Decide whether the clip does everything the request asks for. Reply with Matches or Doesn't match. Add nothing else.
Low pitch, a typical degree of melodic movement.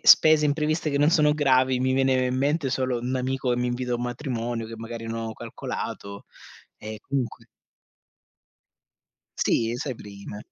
Matches